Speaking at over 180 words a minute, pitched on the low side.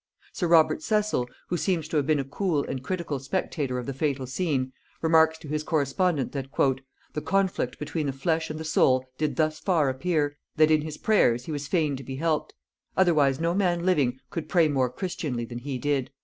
No: fast, 205 wpm; medium, 155 Hz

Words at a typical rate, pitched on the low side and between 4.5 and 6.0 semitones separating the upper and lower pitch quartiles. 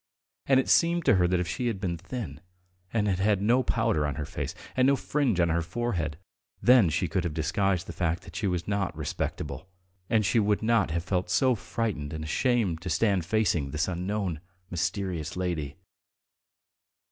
Yes: average, 190 wpm; very low, 95 Hz; average, 4.9 semitones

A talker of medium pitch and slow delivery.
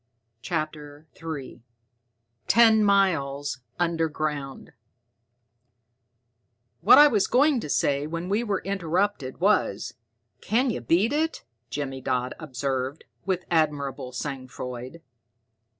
Yes: medium, 155 Hz; slow, 105 wpm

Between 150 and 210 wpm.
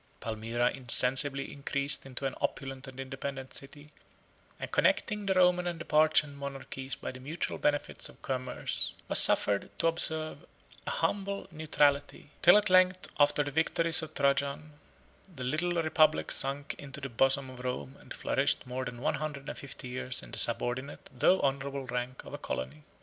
Yes: average, 170 wpm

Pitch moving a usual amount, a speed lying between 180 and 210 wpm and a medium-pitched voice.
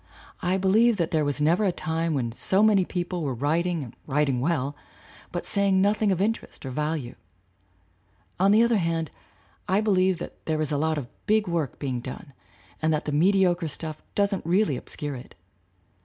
Yes: average, 4.4 semitones; average, 185 wpm; medium, 165 Hz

